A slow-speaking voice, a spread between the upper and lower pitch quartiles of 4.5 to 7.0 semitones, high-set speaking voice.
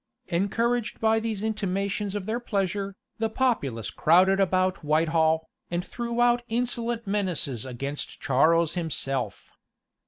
Yes: slow, 120 wpm; wide, 5.6 semitones; high, 195 Hz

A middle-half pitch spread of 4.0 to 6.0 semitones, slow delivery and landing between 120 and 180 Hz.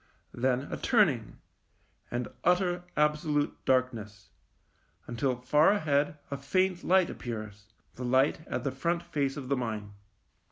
Yes: average, 5.3 semitones; slow, 130 wpm; medium, 140 Hz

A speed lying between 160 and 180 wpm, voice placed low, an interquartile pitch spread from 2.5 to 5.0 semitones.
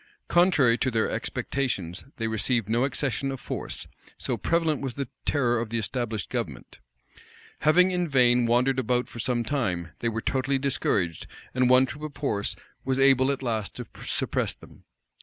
Yes: average, 170 wpm; low, 125 Hz; average, 3.1 semitones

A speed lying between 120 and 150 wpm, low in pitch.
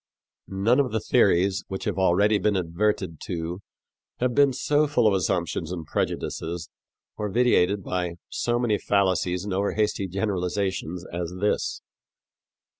Yes: average, 140 wpm; very low, 95 Hz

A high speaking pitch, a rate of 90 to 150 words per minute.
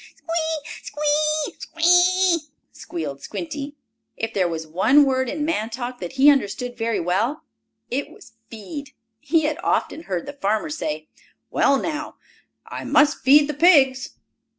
Yes: very high, 280 Hz; average, 145 wpm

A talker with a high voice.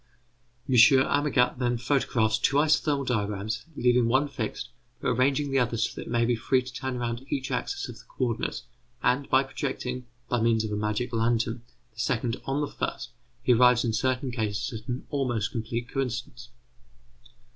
No: low, 125 Hz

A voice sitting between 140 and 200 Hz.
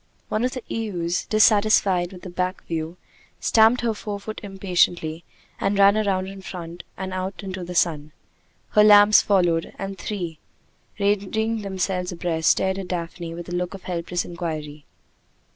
Yes: medium, 185 Hz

